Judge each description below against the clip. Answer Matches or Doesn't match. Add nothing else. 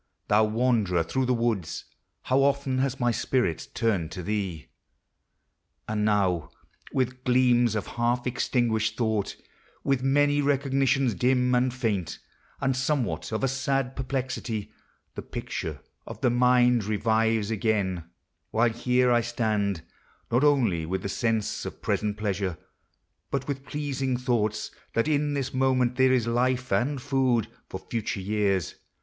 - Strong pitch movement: Doesn't match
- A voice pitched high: Doesn't match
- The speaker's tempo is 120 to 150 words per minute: Matches